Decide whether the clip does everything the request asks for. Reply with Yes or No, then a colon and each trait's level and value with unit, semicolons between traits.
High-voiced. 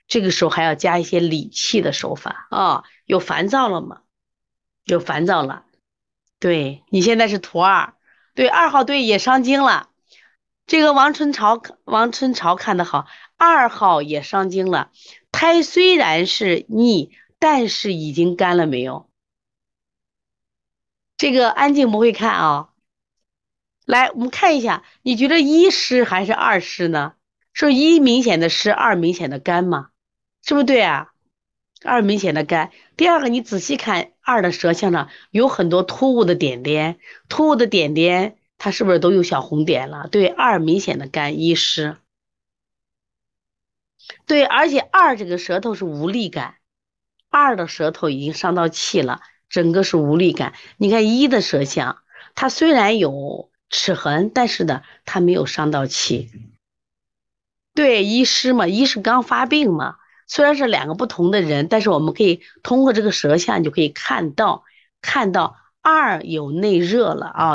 Yes: high, 195 Hz